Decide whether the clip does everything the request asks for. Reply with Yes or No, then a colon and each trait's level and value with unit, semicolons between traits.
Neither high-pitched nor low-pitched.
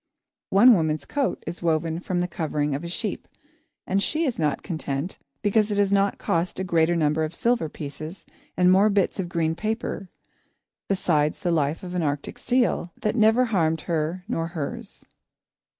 Yes: medium, 175 Hz